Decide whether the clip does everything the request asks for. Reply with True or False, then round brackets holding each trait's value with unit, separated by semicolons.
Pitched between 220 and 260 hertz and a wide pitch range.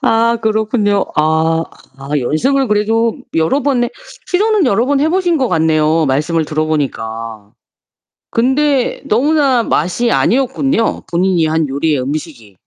False (205 Hz; 8.8 semitones)